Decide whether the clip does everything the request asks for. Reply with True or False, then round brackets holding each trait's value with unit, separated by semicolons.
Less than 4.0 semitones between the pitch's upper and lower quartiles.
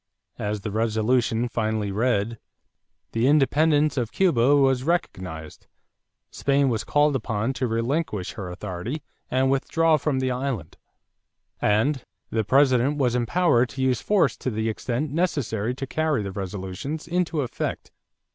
False (4.7 semitones)